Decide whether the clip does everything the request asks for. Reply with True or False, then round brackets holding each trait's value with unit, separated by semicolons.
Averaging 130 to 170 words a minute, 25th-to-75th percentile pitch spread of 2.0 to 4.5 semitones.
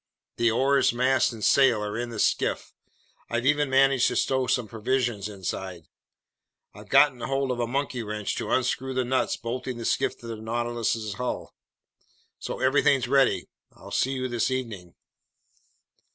True (160 wpm; 2.8 semitones)